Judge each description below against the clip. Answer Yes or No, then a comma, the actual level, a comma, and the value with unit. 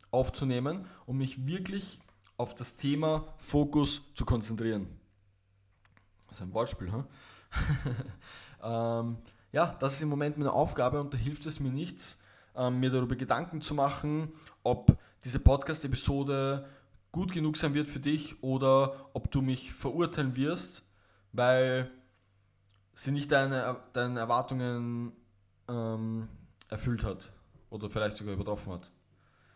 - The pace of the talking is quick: No, average, 130 wpm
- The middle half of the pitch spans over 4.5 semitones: Yes, average, 5.2 semitones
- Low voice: Yes, low, 125 Hz